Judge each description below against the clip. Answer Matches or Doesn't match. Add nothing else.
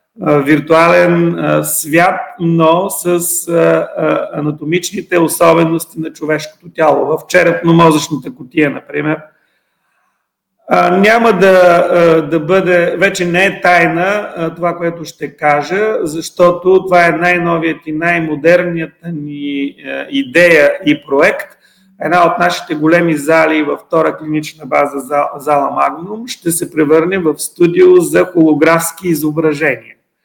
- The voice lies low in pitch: Doesn't match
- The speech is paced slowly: Matches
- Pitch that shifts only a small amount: Matches